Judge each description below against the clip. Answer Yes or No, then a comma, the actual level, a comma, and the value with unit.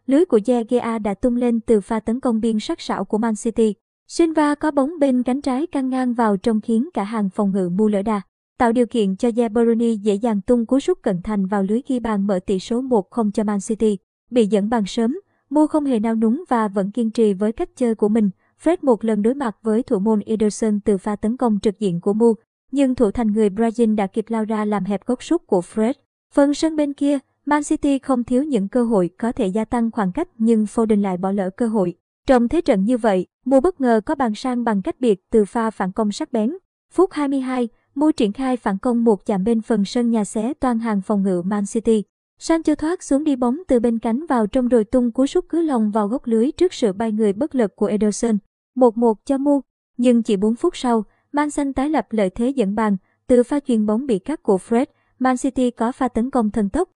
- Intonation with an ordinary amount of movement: Yes, average, 3.2 semitones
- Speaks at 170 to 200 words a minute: No, average, 245 wpm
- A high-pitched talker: Yes, high, 230 Hz